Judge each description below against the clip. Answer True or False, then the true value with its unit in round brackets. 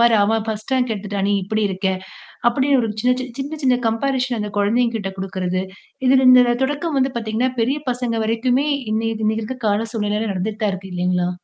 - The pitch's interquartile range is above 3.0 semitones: True (3.5 semitones)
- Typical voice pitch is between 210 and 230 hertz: True (225 Hz)